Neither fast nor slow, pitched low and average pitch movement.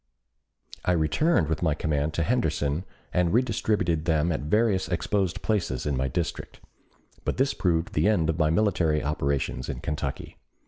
Yes: average, 155 wpm; very low, 80 Hz; average, 4.4 semitones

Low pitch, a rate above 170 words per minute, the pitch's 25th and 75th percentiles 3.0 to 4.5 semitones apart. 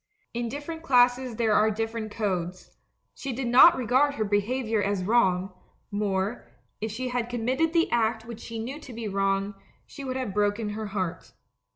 No: high, 225 Hz; average, 185 wpm; average, 3.5 semitones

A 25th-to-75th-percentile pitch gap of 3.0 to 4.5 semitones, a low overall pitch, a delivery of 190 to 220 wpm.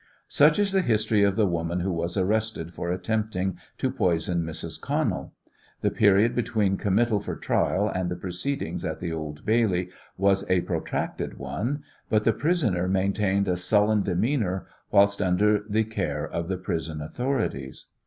No: average, 3.6 semitones; very low, 95 Hz; average, 160 wpm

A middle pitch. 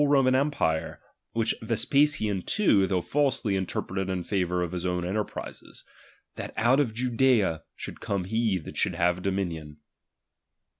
No: low, 100 Hz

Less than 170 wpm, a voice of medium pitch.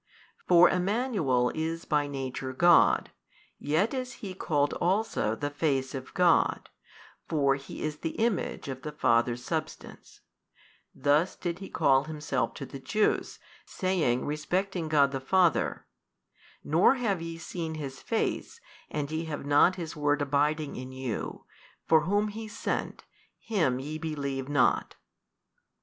Yes: average, 140 wpm; medium, 155 Hz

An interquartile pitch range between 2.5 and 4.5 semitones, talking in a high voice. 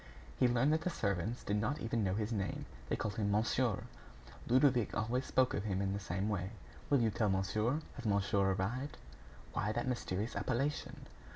No: average, 3.9 semitones; low, 110 Hz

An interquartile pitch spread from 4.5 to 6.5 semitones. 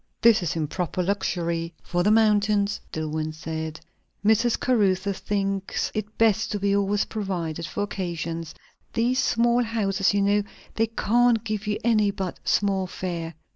No: average, 3.7 semitones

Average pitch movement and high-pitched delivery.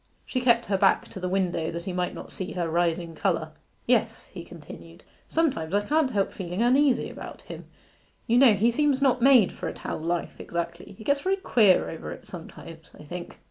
No: wide, 6.7 semitones; high, 195 Hz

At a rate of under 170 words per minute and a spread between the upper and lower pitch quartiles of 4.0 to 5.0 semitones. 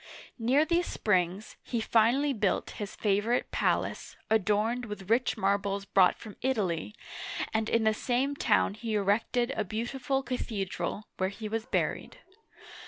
No: average, 140 wpm; average, 3.4 semitones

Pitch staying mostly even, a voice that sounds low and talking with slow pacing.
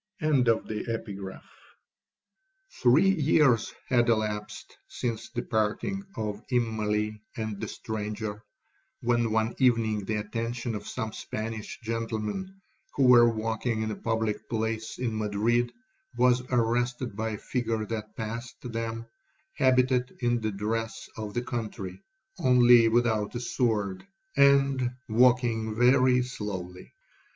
Yes: narrow, 2.3 semitones; low, 115 Hz; slow, 115 wpm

